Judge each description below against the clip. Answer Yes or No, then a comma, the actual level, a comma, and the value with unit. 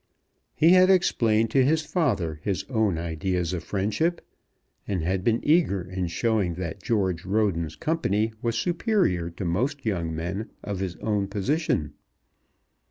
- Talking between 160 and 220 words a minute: No, average, 145 wpm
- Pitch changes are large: Yes, wide, 7.0 semitones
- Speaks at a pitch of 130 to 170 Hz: No, low, 100 Hz